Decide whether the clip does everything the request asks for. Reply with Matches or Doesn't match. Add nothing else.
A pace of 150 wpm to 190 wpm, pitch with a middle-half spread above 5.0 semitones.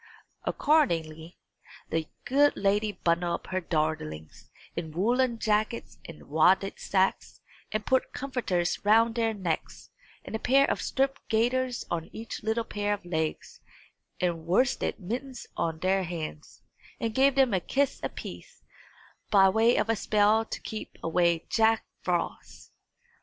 Doesn't match